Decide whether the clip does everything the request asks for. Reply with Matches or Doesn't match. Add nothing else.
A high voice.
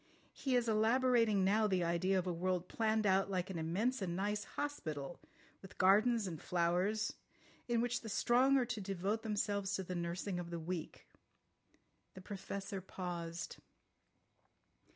Matches